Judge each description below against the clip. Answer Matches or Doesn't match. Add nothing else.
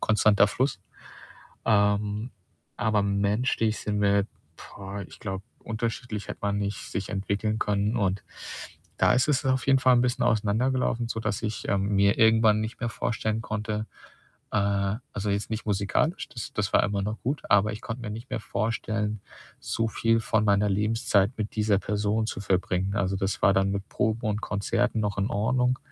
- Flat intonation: Matches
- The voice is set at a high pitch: Doesn't match